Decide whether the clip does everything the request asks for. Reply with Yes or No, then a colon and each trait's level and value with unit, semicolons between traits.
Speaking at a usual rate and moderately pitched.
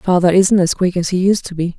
No: fast, 300 wpm; medium, 180 Hz